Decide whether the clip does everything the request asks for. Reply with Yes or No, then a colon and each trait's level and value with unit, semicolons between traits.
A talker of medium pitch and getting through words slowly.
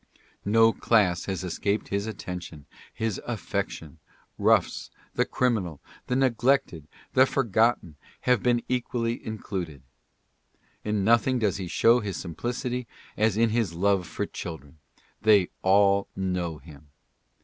No: low, 100 Hz; slow, 125 wpm